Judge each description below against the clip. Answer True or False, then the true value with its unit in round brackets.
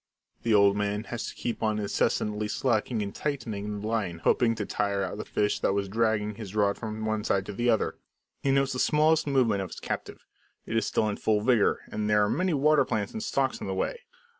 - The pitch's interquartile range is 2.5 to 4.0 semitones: True (2.8 semitones)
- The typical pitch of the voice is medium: False (110 Hz)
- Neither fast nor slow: False (230 wpm)